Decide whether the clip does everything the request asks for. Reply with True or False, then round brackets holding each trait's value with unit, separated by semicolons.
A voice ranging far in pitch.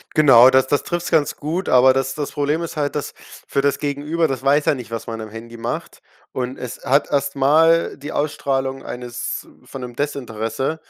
False (2.8 semitones)